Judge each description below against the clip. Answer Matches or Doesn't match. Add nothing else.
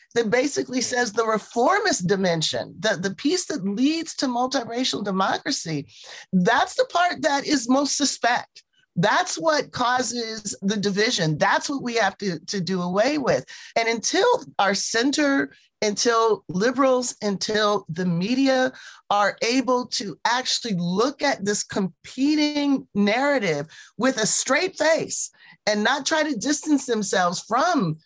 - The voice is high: Matches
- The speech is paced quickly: Doesn't match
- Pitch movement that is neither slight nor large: Doesn't match